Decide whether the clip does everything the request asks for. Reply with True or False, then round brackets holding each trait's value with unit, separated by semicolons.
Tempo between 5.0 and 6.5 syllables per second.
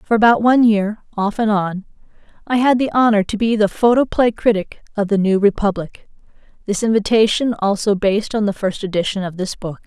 True (5.5 syllables/s)